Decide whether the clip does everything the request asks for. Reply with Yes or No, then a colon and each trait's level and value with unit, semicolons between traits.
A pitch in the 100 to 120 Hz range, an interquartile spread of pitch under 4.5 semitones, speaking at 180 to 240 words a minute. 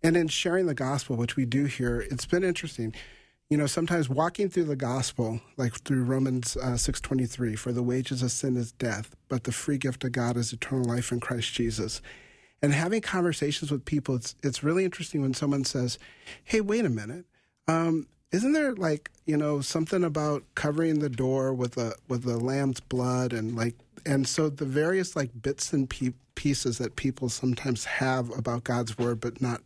No: low, 130 Hz; average, 3.5 semitones; average, 200 wpm